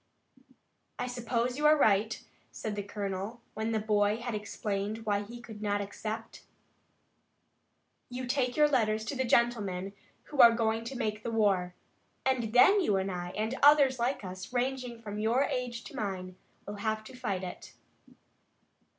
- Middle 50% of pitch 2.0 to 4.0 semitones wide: Yes, average, 3.3 semitones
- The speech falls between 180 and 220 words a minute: No, average, 165 wpm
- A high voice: Yes, high, 220 Hz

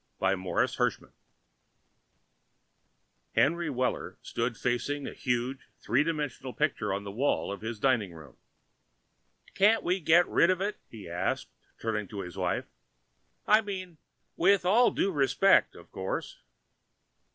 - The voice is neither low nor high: No, low, 130 Hz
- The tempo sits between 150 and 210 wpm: No, slow, 135 wpm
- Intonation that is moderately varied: No, wide, 8.5 semitones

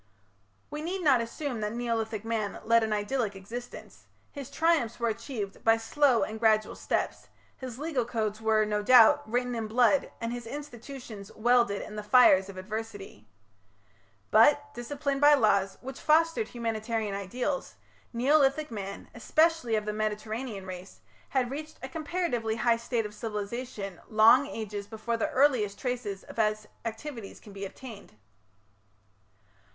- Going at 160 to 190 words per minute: No, average, 145 wpm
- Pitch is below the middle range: No, high, 230 Hz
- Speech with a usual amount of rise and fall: Yes, average, 3.6 semitones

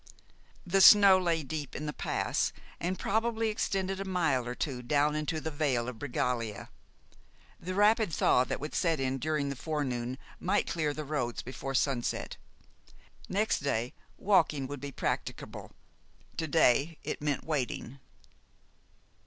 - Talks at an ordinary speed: Yes, average, 145 wpm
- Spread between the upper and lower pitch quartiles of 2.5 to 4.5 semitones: No, average, 5.3 semitones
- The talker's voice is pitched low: No, medium, 150 Hz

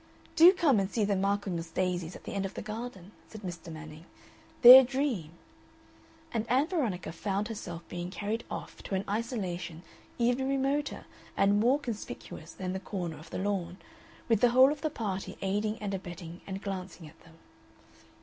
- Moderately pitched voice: No, high, 200 Hz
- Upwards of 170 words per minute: Yes, average, 180 wpm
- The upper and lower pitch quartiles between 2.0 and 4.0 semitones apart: No, average, 4.9 semitones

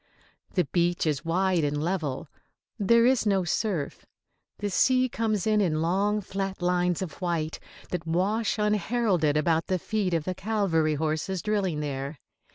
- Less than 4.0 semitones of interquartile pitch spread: No, average, 4.4 semitones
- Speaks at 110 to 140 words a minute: No, average, 155 wpm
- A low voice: No, medium, 180 Hz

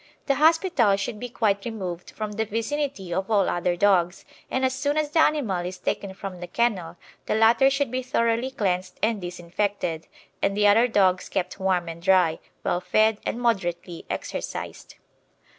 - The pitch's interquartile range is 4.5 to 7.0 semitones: Yes, average, 4.8 semitones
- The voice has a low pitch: No, high, 205 Hz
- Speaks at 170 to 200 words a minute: Yes, average, 175 wpm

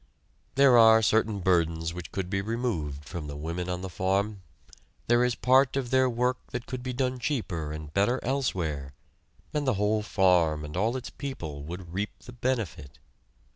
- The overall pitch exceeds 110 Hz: No, low, 100 Hz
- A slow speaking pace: No, average, 175 wpm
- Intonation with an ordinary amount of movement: No, wide, 6.7 semitones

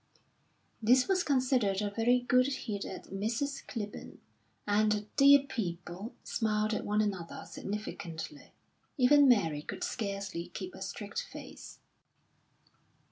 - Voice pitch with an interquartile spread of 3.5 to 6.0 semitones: Yes, average, 4.4 semitones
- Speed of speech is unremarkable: No, slow, 125 wpm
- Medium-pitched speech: No, high, 215 Hz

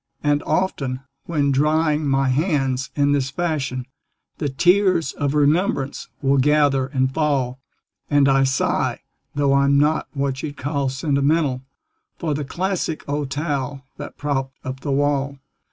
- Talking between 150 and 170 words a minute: No, average, 140 wpm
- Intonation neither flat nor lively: No, narrow, 2.0 semitones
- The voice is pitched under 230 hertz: Yes, medium, 140 Hz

